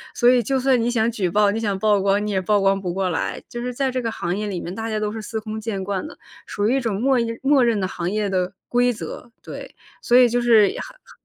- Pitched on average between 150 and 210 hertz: No, high, 220 Hz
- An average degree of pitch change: Yes, average, 3.5 semitones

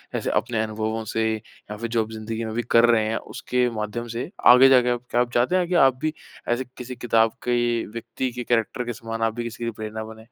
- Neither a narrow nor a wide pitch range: No, narrow, 1.6 semitones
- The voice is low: Yes, low, 115 Hz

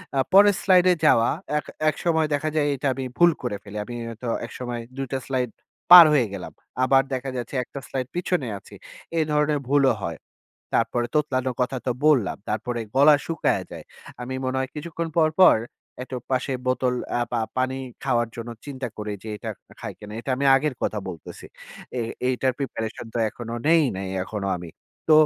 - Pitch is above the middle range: No, low, 130 Hz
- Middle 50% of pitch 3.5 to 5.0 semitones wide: Yes, average, 3.8 semitones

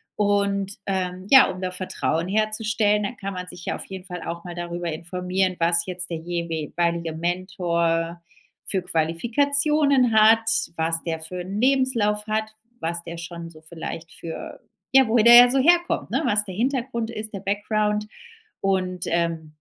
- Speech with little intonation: No, average, 4.2 semitones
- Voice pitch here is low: No, medium, 185 Hz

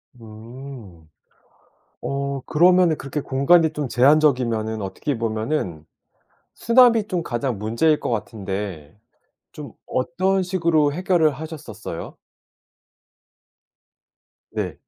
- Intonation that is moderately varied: No, wide, 6.5 semitones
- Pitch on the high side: No, medium, 140 Hz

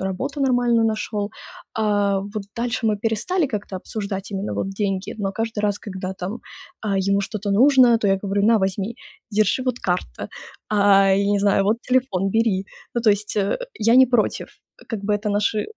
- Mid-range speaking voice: No, high, 210 Hz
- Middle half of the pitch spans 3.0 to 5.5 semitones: No, narrow, 2.6 semitones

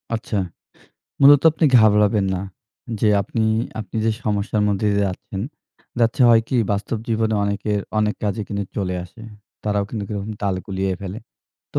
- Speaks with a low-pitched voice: Yes, low, 105 Hz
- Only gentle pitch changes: Yes, narrow, 1.8 semitones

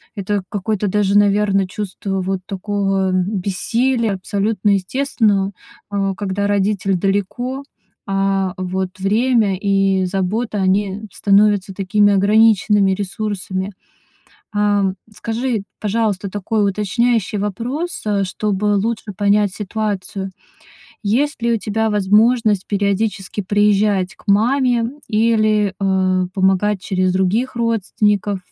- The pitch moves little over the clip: Yes, narrow, 1.9 semitones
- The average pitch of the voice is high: Yes, high, 205 Hz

